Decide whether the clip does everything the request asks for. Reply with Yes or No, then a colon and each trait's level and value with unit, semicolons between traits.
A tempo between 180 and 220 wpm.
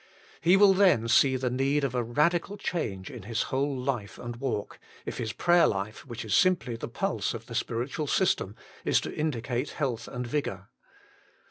Yes: average, 185 wpm